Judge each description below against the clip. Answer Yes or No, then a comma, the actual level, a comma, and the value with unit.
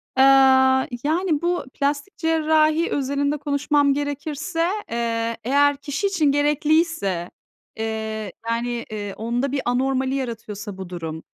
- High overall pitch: Yes, very high, 275 Hz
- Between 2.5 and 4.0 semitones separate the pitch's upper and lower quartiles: No, average, 4.5 semitones